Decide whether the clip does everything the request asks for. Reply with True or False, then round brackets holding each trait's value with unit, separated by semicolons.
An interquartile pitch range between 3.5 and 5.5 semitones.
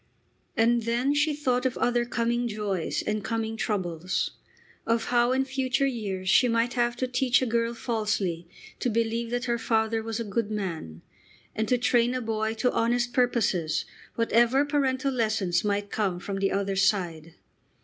False (3.0 semitones)